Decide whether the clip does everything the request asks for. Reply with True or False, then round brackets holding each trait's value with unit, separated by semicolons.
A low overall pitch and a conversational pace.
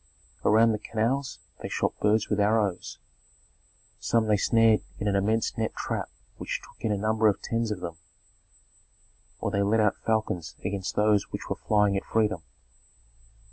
True (105 Hz; 165 wpm)